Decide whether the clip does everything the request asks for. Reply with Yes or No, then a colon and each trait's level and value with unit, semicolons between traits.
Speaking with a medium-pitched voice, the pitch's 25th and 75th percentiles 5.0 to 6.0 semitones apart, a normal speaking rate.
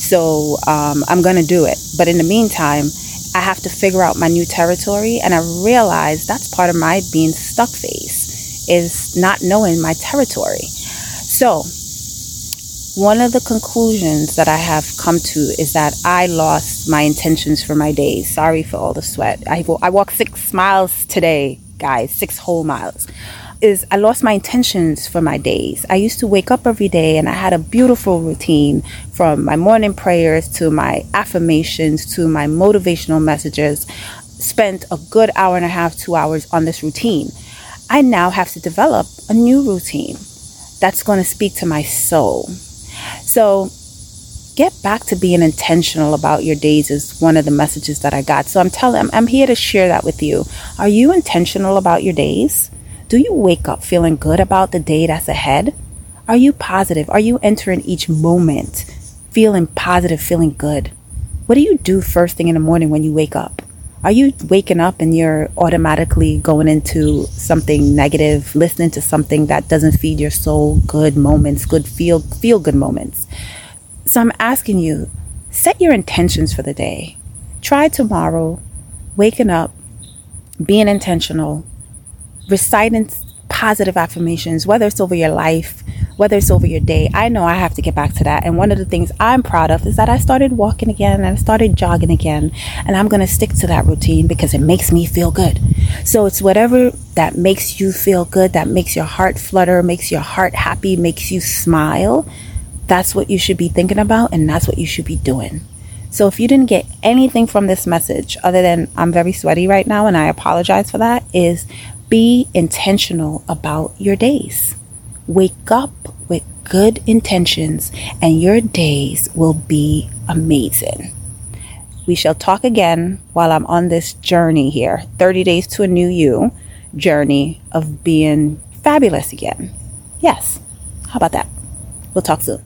No: medium, 170 Hz; average, 4.6 semitones; average, 180 wpm